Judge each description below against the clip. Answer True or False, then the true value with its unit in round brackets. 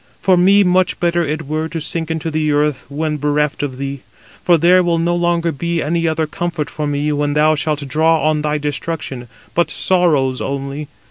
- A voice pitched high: False (155 Hz)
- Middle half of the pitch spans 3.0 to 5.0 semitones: False (2.6 semitones)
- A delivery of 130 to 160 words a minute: False (195 wpm)